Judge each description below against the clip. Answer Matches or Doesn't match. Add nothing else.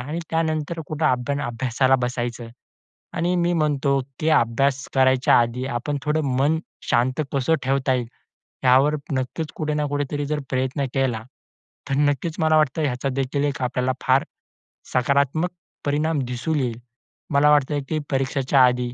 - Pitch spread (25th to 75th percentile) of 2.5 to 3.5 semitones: Matches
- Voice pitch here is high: Doesn't match